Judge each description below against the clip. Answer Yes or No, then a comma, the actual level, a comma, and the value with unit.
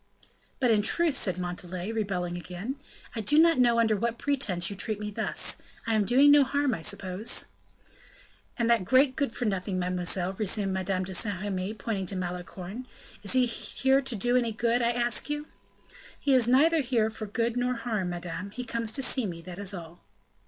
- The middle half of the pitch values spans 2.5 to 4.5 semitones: No, average, 5.0 semitones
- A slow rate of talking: No, average, 195 wpm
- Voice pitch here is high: Yes, high, 220 Hz